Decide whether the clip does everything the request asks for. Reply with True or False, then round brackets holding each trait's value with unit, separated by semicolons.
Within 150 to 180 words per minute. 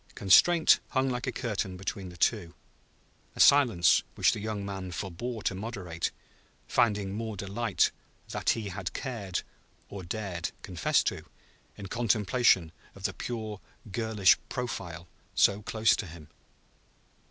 False (135 wpm)